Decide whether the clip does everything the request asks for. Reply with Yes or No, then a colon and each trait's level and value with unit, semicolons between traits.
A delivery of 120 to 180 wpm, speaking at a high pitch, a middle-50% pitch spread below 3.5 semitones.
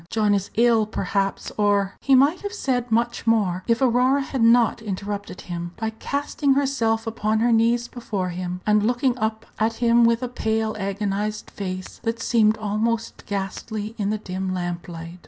Yes: average, 175 wpm; high, 220 Hz; average, 2.9 semitones